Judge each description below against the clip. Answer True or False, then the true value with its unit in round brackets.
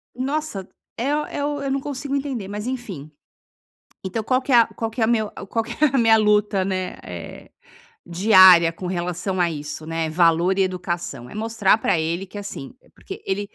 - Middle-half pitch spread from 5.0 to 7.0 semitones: True (5.3 semitones)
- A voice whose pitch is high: True (205 Hz)